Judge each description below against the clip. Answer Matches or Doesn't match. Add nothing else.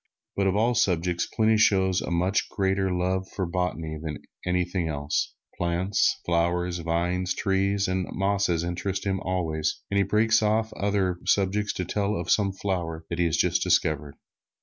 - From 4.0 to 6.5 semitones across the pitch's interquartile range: Doesn't match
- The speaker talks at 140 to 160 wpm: Doesn't match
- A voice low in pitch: Matches